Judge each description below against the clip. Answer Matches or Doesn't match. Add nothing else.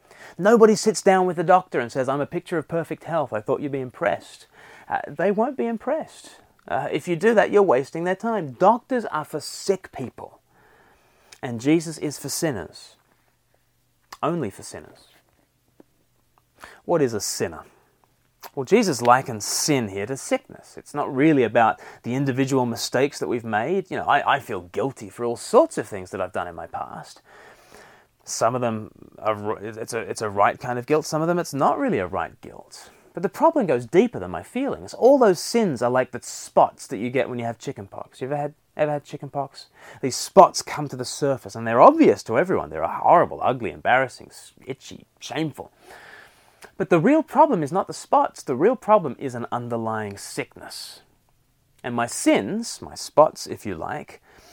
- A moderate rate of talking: Matches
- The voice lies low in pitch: Doesn't match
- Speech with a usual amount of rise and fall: Doesn't match